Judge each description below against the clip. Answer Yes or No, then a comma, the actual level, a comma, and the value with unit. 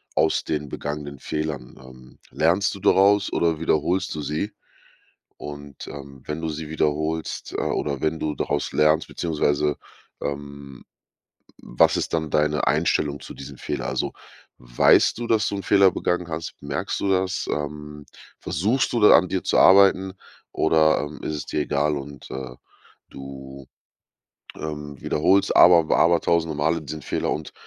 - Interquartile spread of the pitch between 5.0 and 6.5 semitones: No, average, 2.8 semitones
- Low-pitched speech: Yes, very low, 75 Hz